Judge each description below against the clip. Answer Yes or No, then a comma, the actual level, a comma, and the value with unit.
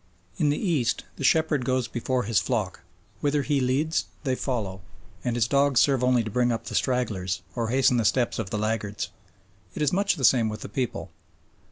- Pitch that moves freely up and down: No, average, 3.7 semitones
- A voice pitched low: Yes, low, 125 Hz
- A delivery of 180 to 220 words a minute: Yes, average, 200 wpm